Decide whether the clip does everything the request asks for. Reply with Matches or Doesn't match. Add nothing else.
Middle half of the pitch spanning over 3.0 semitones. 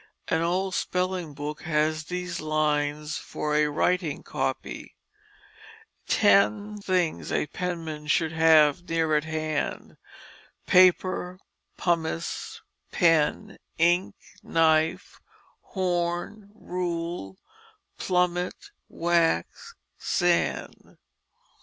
Doesn't match